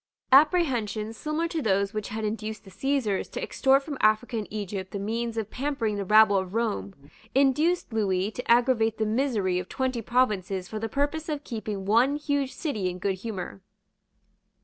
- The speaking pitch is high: Yes, high, 220 Hz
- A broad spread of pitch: No, average, 4.9 semitones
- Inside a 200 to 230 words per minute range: No, average, 175 wpm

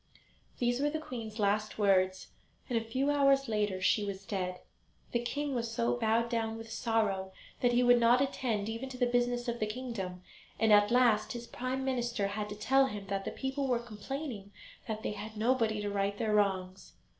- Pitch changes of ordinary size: Yes, average, 3.1 semitones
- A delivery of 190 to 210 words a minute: Yes, average, 200 wpm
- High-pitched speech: Yes, high, 225 Hz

